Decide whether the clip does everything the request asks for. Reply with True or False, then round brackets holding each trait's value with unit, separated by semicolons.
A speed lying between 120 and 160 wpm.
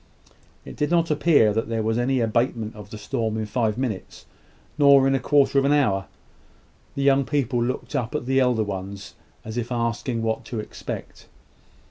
False (185 wpm)